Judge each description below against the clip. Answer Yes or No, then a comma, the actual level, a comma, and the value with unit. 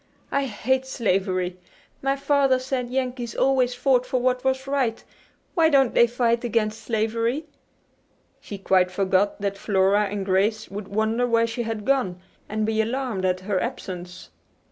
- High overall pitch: Yes, high, 230 Hz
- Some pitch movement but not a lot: Yes, average, 4.4 semitones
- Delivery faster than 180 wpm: No, average, 155 wpm